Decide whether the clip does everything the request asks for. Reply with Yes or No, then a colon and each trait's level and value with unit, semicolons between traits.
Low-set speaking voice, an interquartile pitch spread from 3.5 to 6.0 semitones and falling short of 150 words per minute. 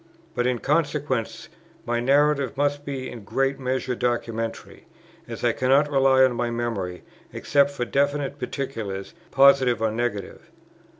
No: low, 130 Hz; average, 2.9 semitones; slow, 135 wpm